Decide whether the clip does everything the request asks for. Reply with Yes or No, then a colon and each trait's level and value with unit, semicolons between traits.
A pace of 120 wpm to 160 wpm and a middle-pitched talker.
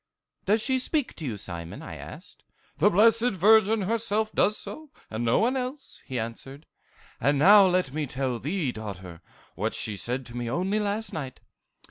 No: average, 175 wpm; medium, 180 Hz